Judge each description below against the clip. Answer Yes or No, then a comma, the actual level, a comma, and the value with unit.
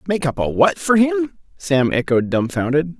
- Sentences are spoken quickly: No, average, 180 wpm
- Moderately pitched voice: Yes, medium, 160 Hz